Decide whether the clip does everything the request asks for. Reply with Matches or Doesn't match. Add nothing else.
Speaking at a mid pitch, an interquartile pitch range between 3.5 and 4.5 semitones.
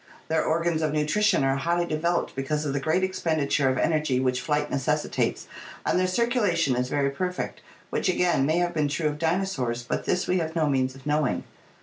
Matches